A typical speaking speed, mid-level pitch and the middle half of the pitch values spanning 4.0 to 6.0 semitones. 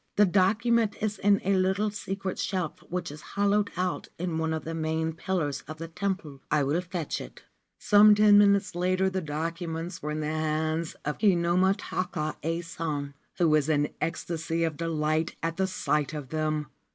No: average, 180 wpm; medium, 165 Hz; average, 3.5 semitones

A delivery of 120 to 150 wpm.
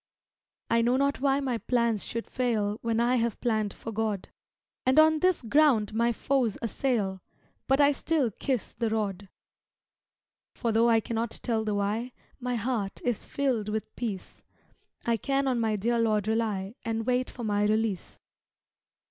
No: average, 165 wpm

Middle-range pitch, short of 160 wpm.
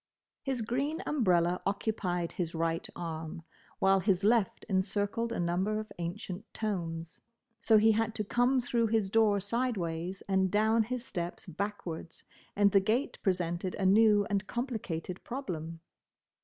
No: high, 200 Hz; average, 140 wpm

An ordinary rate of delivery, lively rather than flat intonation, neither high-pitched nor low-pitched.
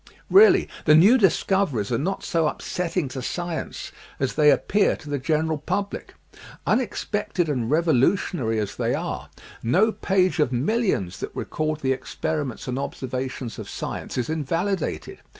Yes: average, 150 wpm; wide, 6.0 semitones; medium, 155 Hz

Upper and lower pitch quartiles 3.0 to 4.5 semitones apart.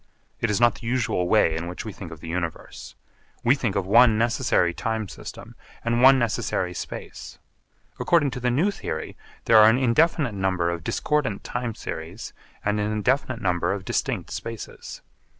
No: average, 5.3 semitones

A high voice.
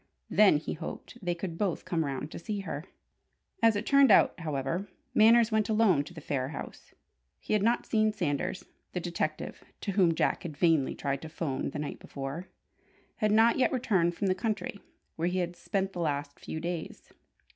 No: medium, 175 Hz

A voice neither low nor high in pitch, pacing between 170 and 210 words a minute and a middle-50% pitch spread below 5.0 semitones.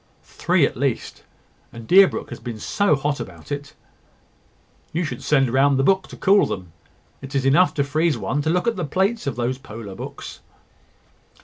No: medium, 145 Hz; average, 190 wpm; average, 5.3 semitones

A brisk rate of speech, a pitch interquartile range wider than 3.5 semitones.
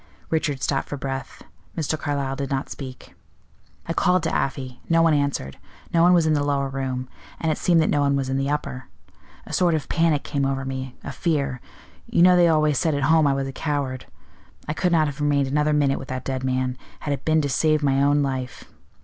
No: fast, 225 wpm; average, 2.7 semitones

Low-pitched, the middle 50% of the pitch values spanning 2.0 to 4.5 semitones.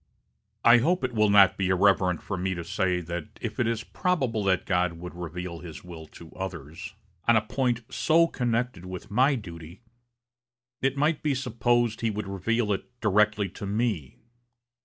No: low, 100 Hz; average, 5.1 semitones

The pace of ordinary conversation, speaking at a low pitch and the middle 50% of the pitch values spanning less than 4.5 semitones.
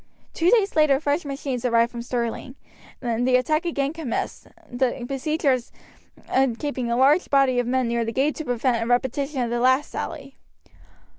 No: average, 170 wpm; very high, 260 Hz; average, 3.0 semitones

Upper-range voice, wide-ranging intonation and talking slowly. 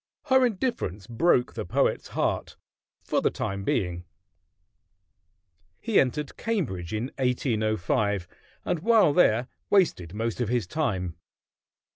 No: low, 115 Hz; wide, 8.6 semitones; slow, 115 wpm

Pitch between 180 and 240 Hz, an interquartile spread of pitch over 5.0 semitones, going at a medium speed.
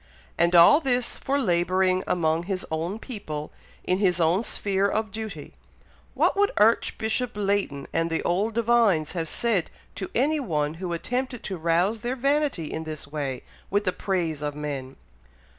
Yes: high, 190 Hz; wide, 5.6 semitones; average, 160 wpm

